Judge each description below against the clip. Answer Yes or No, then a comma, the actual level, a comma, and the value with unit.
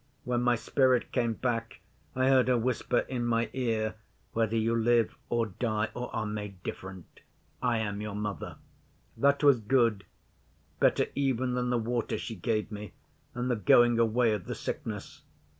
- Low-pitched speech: Yes, low, 115 Hz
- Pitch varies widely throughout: No, narrow, 2.4 semitones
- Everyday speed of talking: Yes, average, 165 wpm